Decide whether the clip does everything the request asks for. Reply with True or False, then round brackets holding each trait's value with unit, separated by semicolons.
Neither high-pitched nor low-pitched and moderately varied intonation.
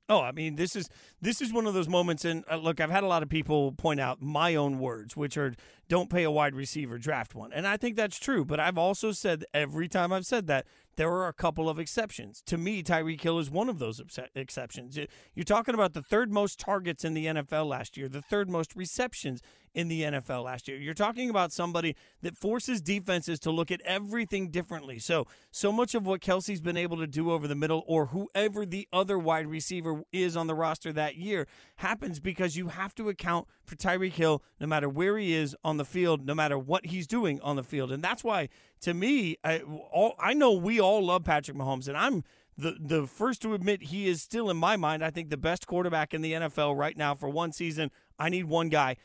True (165 Hz; 3.9 semitones)